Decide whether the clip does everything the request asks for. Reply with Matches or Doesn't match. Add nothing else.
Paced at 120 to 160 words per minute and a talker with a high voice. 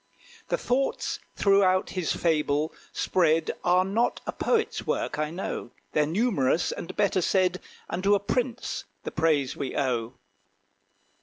Doesn't match